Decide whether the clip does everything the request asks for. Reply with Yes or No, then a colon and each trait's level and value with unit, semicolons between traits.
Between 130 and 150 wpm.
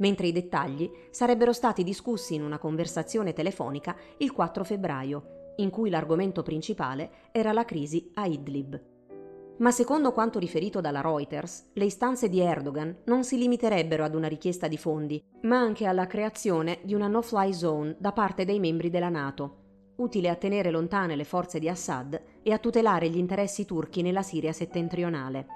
No: average, 165 wpm